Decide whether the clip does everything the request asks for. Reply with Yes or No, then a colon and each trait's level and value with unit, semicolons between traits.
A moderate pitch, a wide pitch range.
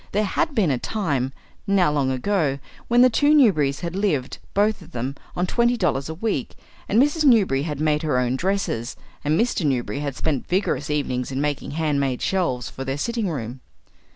Yes: medium, 155 Hz; wide, 7.0 semitones